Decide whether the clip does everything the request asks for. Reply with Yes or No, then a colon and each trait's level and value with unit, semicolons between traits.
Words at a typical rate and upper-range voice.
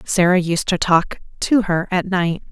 No: average, 190 wpm; medium, 180 Hz